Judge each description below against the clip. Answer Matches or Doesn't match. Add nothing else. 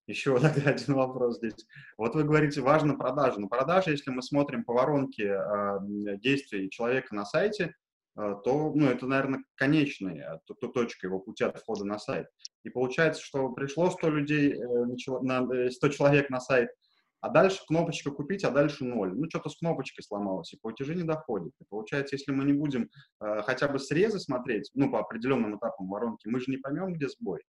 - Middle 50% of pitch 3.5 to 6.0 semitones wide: Matches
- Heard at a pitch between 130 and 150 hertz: Matches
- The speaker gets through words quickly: Matches